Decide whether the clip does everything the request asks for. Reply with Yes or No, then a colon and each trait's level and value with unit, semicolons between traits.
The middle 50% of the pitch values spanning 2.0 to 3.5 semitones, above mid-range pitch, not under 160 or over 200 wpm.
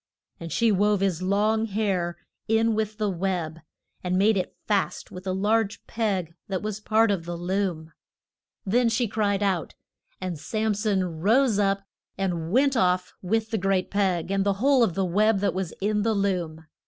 Yes: average, 2.9 semitones; high, 195 Hz; average, 180 wpm